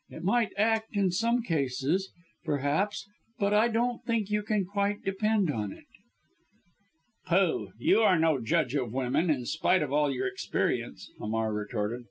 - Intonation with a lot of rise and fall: Yes, wide, 7.5 semitones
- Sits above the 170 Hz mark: Yes, high, 190 Hz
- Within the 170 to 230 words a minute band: No, average, 160 wpm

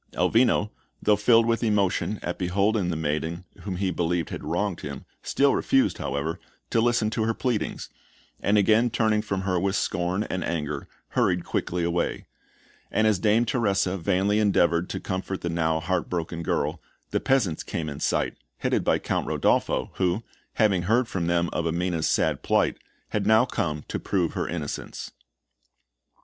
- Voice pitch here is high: No, very low, 95 Hz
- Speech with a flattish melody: No, average, 4.1 semitones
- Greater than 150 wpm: Yes, average, 165 wpm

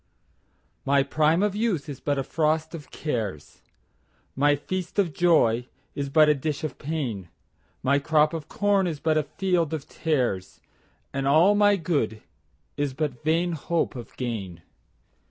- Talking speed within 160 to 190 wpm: No, average, 145 wpm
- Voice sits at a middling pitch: Yes, medium, 150 Hz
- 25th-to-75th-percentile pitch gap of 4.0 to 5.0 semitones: No, average, 3.5 semitones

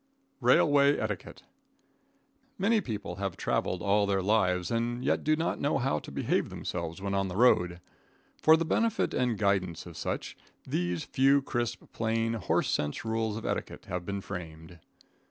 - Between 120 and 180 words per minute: Yes, average, 160 wpm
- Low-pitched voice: Yes, low, 105 Hz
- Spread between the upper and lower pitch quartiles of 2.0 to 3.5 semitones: No, wide, 5.6 semitones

